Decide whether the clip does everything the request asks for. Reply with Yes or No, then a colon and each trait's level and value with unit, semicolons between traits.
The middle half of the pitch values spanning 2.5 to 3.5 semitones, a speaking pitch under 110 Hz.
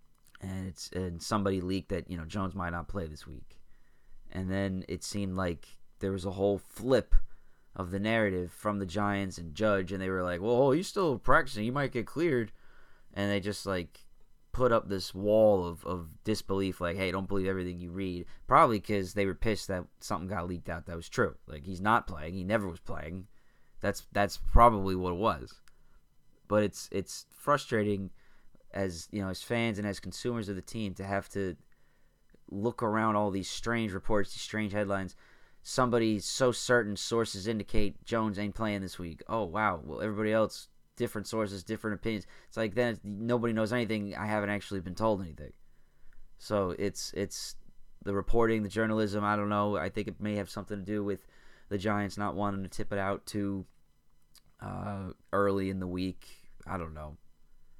Yes: average, 2.9 semitones; low, 100 Hz